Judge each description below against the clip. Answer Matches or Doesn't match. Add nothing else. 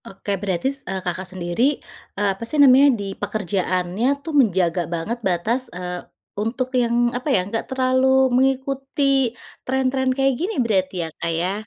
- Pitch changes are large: Matches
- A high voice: Matches